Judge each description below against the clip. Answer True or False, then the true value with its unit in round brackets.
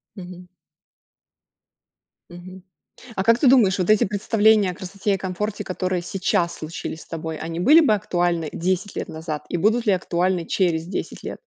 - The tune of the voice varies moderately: True (3.0 semitones)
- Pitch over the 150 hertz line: True (185 Hz)